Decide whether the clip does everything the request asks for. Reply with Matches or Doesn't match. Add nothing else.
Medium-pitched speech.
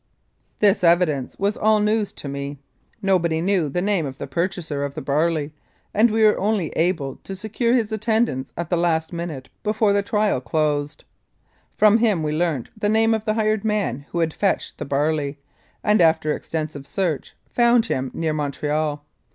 Matches